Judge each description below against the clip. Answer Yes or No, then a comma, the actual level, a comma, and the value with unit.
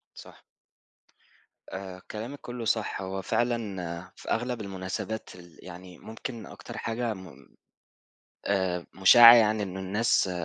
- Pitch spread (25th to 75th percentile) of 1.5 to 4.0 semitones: Yes, average, 3.7 semitones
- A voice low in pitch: Yes, low, 100 Hz